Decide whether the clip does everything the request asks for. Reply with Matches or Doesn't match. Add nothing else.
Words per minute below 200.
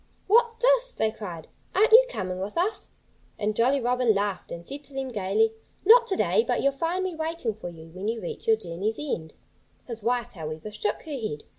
Doesn't match